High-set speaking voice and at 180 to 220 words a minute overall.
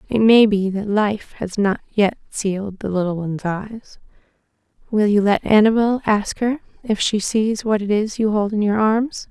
Yes: high, 210 Hz; average, 195 wpm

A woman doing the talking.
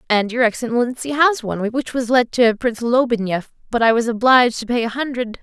Yes: female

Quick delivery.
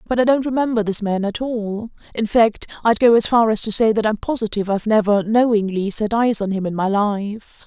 Yes: fast, 210 wpm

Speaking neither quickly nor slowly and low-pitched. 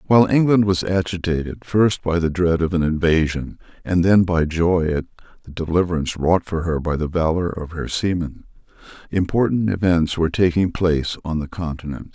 Yes: average, 175 wpm; very low, 85 Hz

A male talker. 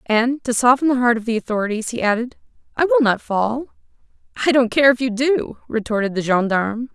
No: female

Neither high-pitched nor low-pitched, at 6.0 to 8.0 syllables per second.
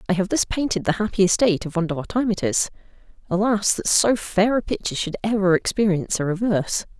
No: high, 195 Hz; 6.3 syllables/s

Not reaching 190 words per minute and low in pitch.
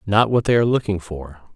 No: fast, 230 wpm; low, 100 Hz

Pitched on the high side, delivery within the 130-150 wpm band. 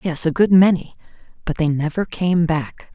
No: medium, 170 Hz; average, 140 wpm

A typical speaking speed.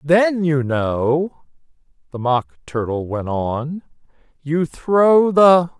No: slow, 115 wpm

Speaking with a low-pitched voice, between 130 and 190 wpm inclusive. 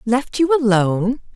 No: high, 240 Hz; slow, 135 wpm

